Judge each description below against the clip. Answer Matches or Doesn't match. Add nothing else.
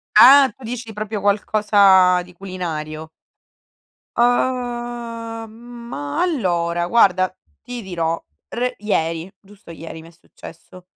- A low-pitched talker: Doesn't match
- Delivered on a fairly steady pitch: Doesn't match